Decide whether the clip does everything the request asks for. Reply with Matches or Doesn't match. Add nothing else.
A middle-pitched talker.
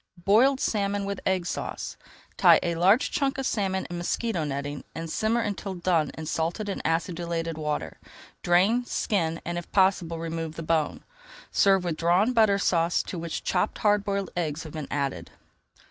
Matches